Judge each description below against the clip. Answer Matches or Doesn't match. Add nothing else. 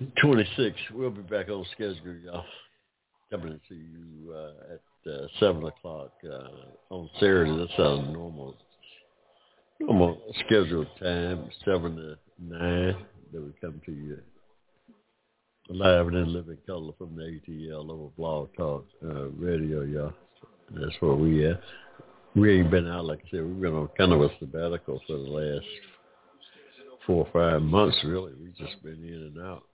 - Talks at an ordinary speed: Matches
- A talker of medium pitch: Doesn't match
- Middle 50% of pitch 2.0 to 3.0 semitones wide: Matches